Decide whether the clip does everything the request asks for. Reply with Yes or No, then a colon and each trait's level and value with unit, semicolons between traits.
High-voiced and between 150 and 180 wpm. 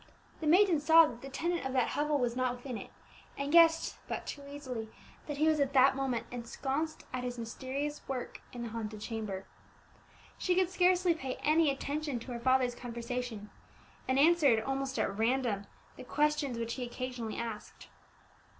Yes: very high, 265 Hz; average, 175 wpm